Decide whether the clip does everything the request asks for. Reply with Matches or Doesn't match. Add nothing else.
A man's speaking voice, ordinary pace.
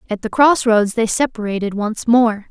Doesn't match